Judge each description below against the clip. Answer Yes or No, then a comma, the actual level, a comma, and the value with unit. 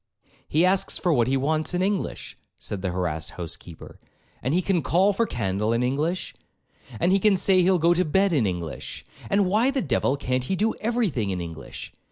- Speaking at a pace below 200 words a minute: No, fast, 205 wpm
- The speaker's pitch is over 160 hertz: No, medium, 155 Hz